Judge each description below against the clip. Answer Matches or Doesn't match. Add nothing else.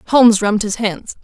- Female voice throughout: Matches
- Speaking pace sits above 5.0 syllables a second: Matches